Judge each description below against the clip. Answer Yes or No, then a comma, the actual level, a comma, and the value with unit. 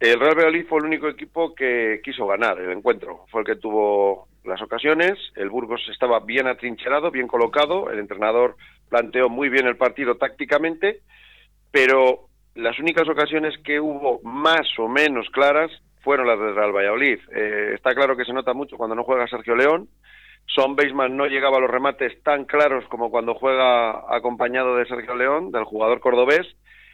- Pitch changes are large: No, average, 4.2 semitones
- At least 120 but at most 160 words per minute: No, average, 175 wpm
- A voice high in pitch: No, low, 130 Hz